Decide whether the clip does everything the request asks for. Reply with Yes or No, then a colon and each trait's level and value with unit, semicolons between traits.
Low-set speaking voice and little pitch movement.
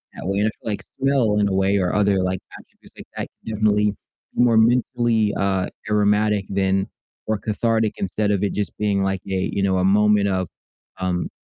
Yes: low, 100 Hz; narrow, 1.8 semitones